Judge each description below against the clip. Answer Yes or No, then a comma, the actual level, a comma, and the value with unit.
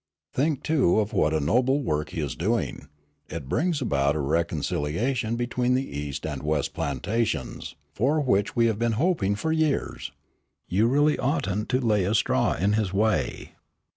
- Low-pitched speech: Yes, low, 110 Hz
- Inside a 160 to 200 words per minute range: Yes, average, 170 wpm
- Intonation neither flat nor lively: No, wide, 8.5 semitones